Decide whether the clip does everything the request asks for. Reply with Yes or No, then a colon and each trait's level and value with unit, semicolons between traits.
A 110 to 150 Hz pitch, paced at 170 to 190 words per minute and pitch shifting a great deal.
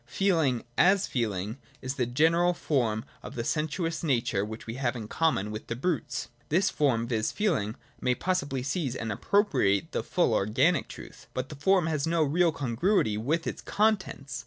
Yes: medium, 140 Hz; average, 175 wpm; wide, 6.3 semitones